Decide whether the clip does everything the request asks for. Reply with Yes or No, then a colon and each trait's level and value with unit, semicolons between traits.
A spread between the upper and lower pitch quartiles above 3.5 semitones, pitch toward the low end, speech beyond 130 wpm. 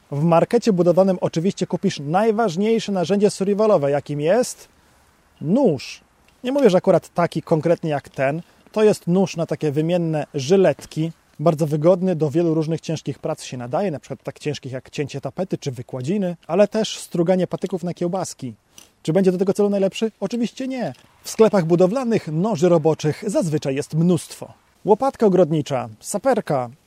No: average, 4.4 semitones; medium, 175 Hz; average, 155 wpm